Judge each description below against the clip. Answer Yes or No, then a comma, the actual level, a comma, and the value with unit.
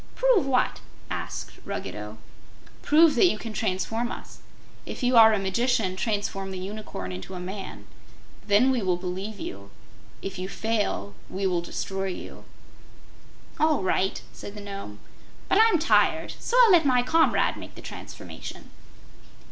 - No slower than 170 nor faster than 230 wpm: No, average, 150 wpm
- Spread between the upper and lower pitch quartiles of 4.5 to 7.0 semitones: Yes, average, 5.1 semitones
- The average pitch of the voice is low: No, high, 205 Hz